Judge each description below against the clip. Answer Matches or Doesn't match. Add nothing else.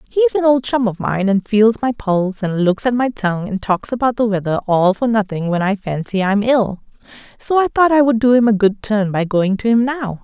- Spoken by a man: Doesn't match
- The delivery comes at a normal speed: Doesn't match